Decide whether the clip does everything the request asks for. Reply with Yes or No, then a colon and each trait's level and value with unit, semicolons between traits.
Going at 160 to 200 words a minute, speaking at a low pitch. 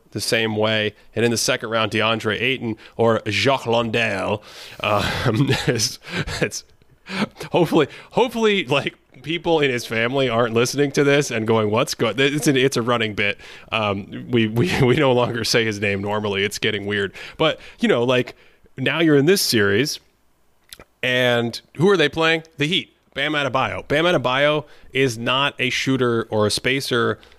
Yes: average, 165 wpm; low, 120 Hz